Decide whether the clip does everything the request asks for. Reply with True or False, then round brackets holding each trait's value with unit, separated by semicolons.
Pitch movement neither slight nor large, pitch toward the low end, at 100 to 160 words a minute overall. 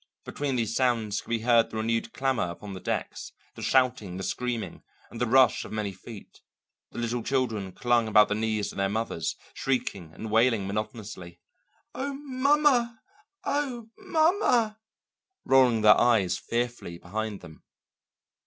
True (4.0 semitones; 115 Hz; 150 wpm)